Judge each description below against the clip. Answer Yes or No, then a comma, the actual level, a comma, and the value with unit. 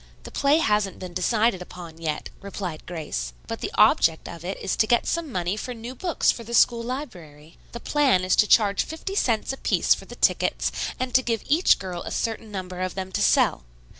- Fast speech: Yes, fast, 215 wpm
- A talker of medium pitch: No, high, 205 Hz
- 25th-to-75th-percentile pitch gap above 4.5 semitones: Yes, average, 5.3 semitones